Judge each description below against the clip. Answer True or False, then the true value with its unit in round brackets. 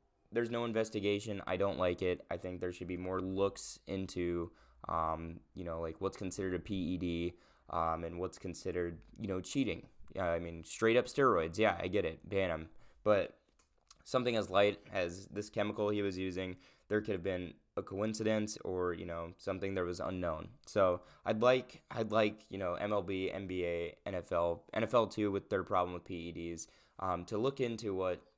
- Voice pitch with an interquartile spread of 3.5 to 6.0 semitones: False (3.0 semitones)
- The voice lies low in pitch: True (95 Hz)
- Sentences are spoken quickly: False (180 wpm)